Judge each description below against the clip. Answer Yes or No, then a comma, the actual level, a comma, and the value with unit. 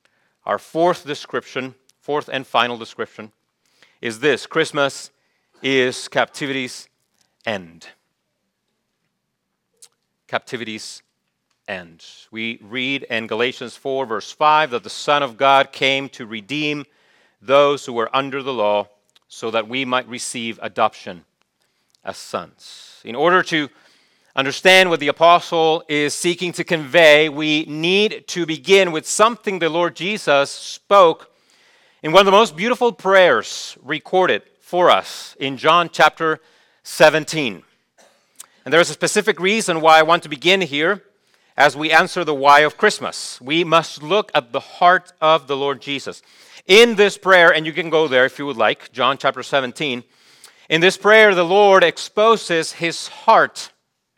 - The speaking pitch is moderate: Yes, medium, 155 Hz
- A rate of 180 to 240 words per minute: No, average, 145 wpm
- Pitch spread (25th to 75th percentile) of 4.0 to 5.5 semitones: Yes, average, 4.6 semitones